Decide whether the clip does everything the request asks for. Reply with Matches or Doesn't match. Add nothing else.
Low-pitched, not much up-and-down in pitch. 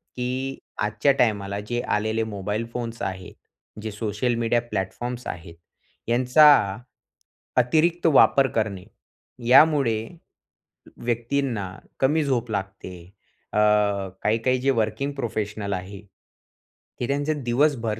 Doesn't match